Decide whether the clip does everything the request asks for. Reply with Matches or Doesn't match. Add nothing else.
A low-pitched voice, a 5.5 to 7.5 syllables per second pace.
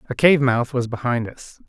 Doesn't match